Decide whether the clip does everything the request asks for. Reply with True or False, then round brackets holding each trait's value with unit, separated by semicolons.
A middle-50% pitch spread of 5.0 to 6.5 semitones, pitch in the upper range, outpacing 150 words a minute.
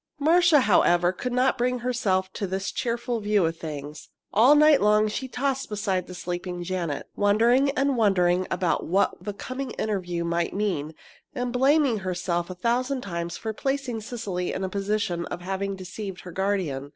True (5.6 semitones; 200 Hz; 170 wpm)